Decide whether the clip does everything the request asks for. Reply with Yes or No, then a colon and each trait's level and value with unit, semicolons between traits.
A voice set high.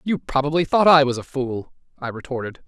No: medium, 140 Hz